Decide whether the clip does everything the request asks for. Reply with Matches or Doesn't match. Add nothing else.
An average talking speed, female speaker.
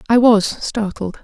Matches